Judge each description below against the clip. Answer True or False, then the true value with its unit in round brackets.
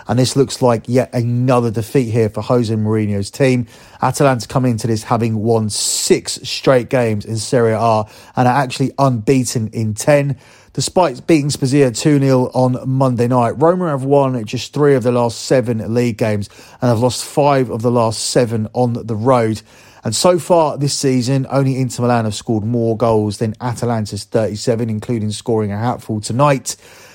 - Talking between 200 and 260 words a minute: False (175 wpm)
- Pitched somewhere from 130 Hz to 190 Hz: False (120 Hz)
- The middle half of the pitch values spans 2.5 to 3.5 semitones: True (2.9 semitones)